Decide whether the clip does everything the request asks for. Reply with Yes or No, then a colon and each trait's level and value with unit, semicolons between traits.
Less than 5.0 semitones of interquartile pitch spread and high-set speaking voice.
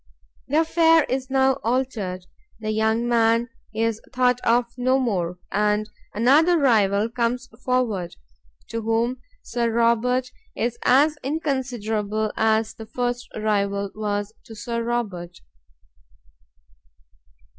Yes: average, 2.9 semitones; high, 230 Hz